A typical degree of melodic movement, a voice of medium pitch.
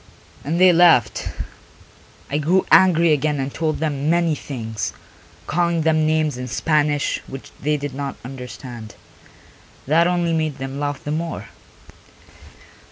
Yes: average, 3.2 semitones; medium, 150 Hz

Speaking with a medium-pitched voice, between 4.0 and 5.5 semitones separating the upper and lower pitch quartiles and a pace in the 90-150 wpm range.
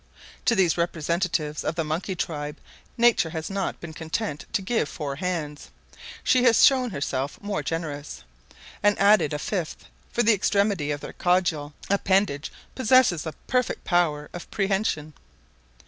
Yes: medium, 175 Hz; average, 5.1 semitones; average, 145 wpm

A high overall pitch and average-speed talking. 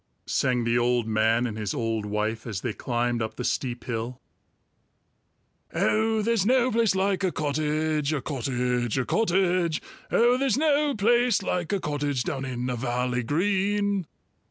No: medium, 145 Hz; average, 155 wpm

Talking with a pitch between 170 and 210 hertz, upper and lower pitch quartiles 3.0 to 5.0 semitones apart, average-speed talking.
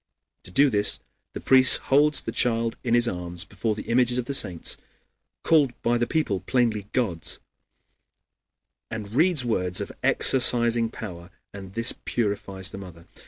No: low, 115 Hz; average, 4.4 semitones; average, 155 wpm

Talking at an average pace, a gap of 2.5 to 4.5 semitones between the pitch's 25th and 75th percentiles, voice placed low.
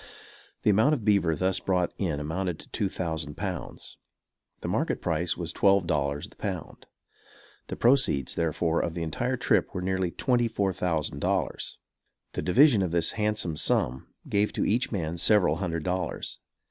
Yes: average, 165 wpm; average, 3.9 semitones; very low, 90 Hz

